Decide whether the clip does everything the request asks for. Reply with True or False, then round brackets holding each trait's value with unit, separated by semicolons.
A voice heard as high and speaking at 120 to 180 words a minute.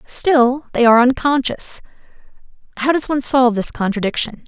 True (255 Hz; 135 wpm)